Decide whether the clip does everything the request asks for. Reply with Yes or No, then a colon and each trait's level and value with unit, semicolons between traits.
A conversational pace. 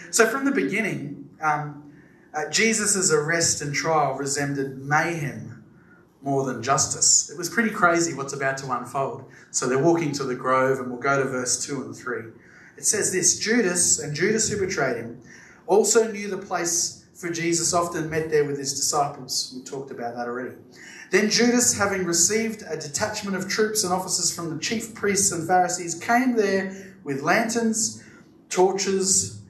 Yes: average, 170 wpm